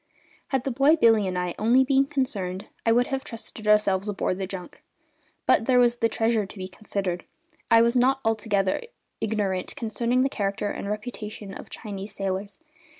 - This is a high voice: Yes, high, 215 Hz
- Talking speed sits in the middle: Yes, average, 180 wpm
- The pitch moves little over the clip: No, average, 3.7 semitones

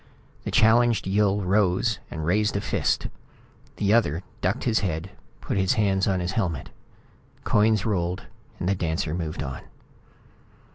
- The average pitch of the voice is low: Yes, very low, 95 Hz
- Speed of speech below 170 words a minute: Yes, average, 140 wpm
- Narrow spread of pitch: No, average, 3.3 semitones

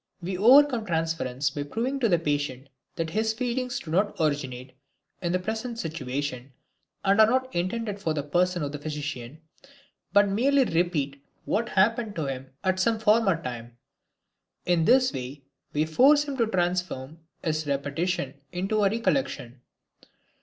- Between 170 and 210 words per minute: No, average, 155 wpm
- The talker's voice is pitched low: No, medium, 175 Hz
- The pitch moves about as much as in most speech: No, wide, 7.4 semitones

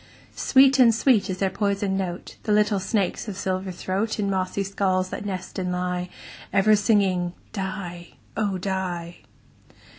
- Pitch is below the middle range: No, high, 190 Hz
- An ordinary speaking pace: Yes, average, 150 wpm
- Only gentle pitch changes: Yes, narrow, 2.0 semitones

